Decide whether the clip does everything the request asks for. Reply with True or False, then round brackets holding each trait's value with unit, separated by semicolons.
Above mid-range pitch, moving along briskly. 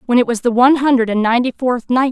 True (245 Hz; 285 wpm)